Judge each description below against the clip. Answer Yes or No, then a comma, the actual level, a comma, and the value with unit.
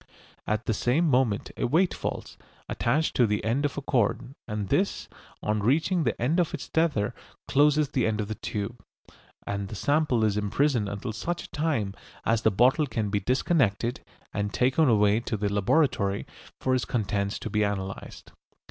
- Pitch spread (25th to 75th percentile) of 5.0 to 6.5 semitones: Yes, wide, 5.6 semitones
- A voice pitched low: Yes, low, 115 Hz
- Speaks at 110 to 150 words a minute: No, average, 175 wpm